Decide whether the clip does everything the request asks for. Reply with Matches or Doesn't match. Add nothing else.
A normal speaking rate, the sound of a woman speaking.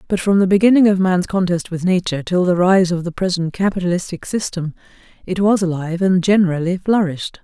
Matches